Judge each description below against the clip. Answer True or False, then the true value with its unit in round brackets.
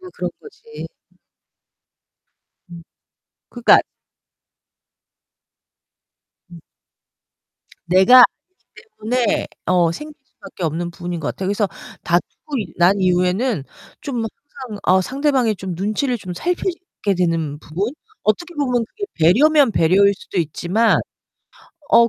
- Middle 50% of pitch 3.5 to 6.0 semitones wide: False (7.1 semitones)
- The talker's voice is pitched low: False (205 Hz)